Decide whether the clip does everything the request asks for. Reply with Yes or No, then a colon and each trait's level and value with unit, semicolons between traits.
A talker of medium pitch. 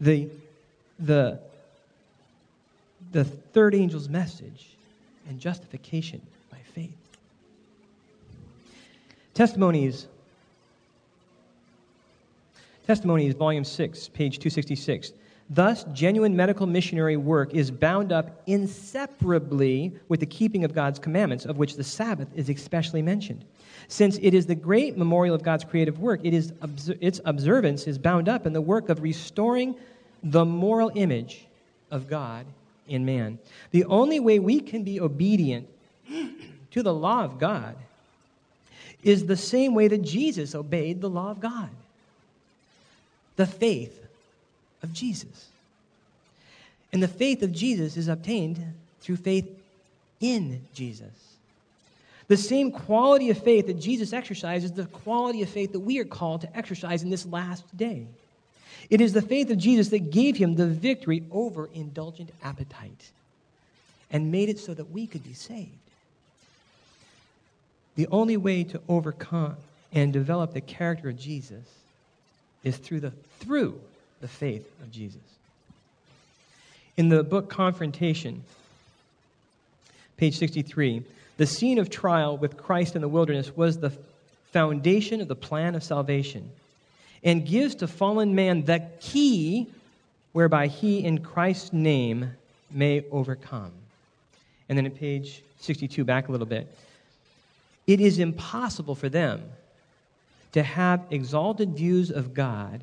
Yes: medium, 165 Hz